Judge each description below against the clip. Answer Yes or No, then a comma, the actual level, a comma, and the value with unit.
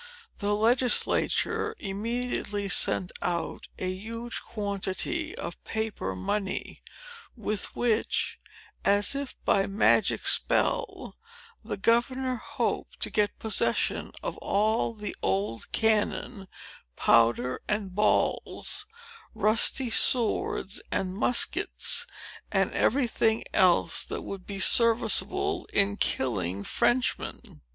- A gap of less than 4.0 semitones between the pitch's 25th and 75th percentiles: Yes, average, 3.4 semitones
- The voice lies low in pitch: No, high, 210 Hz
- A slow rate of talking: Yes, slow, 100 wpm